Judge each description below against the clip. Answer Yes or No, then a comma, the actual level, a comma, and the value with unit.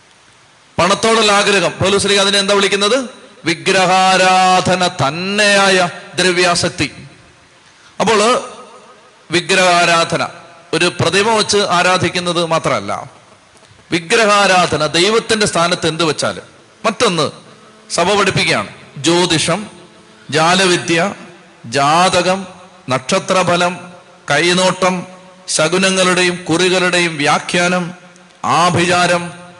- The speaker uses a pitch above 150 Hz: Yes, medium, 180 Hz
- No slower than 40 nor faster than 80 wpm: Yes, slow, 60 wpm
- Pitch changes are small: Yes, narrow, 1.6 semitones